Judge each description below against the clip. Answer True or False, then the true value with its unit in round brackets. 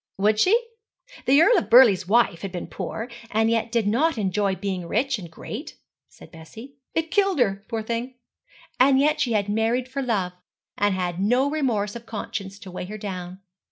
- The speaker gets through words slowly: False (190 wpm)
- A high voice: True (220 Hz)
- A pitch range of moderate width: True (4.7 semitones)